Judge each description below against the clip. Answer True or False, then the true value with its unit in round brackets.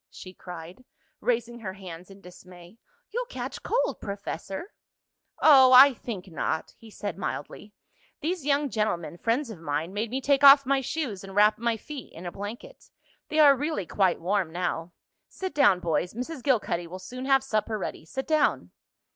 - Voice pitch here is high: True (215 Hz)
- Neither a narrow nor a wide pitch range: False (6.8 semitones)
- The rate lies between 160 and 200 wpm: True (170 wpm)